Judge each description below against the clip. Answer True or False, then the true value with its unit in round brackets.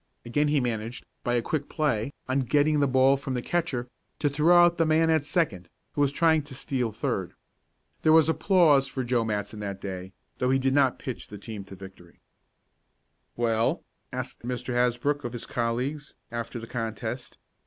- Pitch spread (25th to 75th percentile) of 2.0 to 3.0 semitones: False (4.2 semitones)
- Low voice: True (130 Hz)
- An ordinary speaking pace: True (185 wpm)